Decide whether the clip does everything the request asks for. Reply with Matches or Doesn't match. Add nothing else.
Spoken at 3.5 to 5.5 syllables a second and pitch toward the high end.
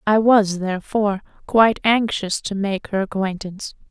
Matches